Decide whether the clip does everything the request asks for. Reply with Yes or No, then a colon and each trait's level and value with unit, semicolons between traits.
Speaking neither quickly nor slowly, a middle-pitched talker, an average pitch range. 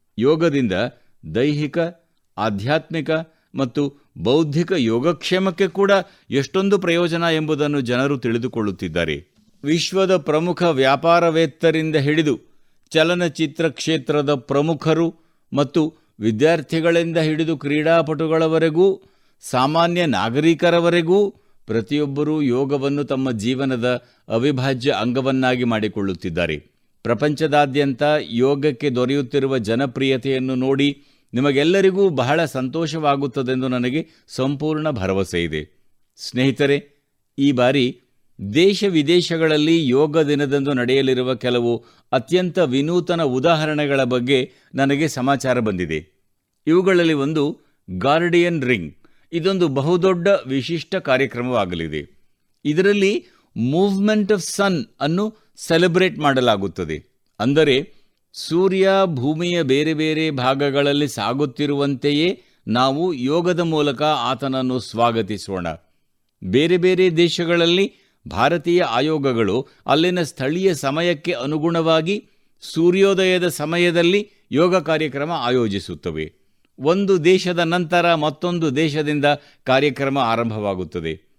Yes: average, 80 wpm; medium, 150 Hz; average, 4.7 semitones